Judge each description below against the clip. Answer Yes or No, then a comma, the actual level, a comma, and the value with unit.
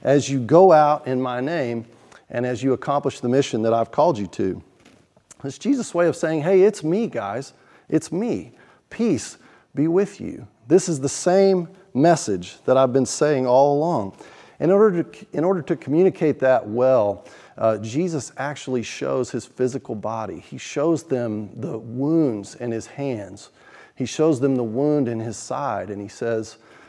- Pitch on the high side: No, low, 135 Hz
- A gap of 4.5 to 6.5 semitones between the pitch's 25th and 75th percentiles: Yes, average, 5.1 semitones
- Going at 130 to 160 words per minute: No, average, 175 wpm